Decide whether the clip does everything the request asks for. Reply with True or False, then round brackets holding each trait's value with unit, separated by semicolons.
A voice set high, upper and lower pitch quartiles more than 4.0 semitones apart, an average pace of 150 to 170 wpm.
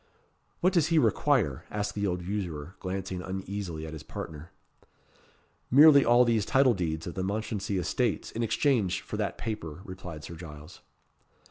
False (95 Hz; 5.3 semitones; 155 wpm)